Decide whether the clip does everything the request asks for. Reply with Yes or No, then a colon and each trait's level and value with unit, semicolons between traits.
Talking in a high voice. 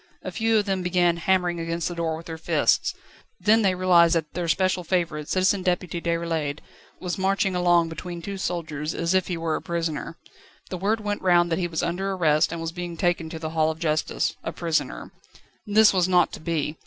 No: medium, 175 Hz